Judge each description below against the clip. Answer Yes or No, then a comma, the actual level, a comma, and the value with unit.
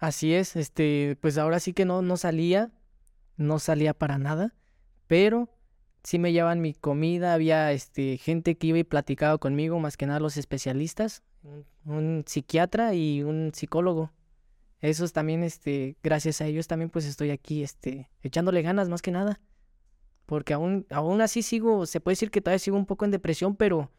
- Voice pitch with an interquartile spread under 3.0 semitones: No, average, 3.4 semitones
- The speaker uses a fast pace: No, average, 175 wpm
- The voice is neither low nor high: Yes, medium, 160 Hz